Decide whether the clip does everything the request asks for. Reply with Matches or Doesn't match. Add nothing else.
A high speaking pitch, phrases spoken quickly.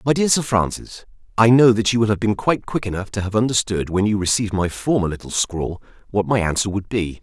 Doesn't match